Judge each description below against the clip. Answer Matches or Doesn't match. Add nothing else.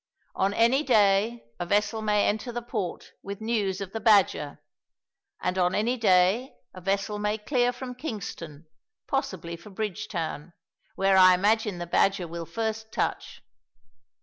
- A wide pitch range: Doesn't match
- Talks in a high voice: Matches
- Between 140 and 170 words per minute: Matches